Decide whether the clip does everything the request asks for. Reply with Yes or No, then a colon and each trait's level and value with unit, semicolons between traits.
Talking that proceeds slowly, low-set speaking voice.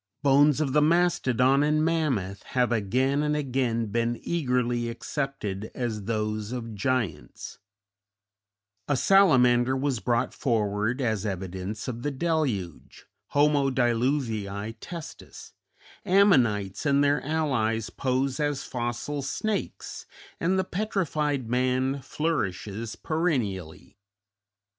Yes: slow, 105 wpm; low, 130 Hz